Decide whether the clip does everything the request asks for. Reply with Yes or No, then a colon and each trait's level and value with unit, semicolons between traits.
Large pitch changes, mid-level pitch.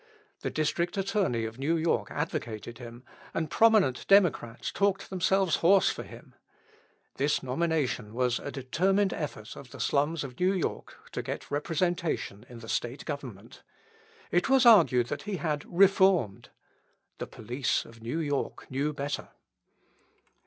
Yes: wide, 6.6 semitones; medium, 150 Hz